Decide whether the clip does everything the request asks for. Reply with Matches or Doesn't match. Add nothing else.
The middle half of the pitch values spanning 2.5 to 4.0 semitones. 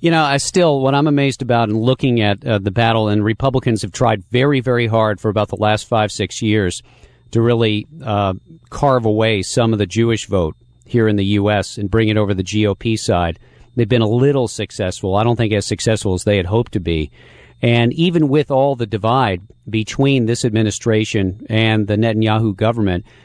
Matches